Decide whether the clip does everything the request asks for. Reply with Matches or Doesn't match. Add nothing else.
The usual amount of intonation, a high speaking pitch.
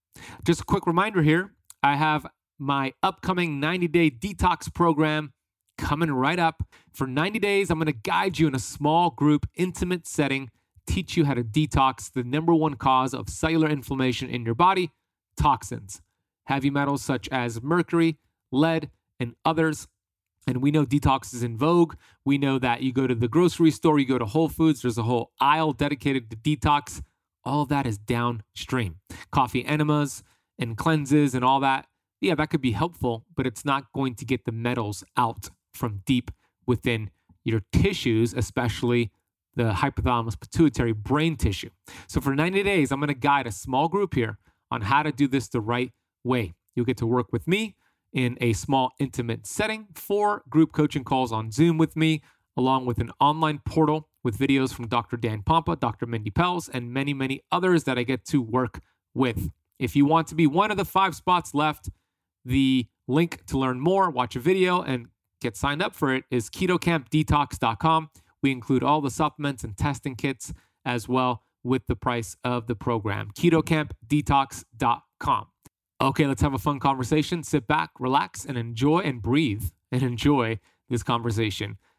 Doesn't match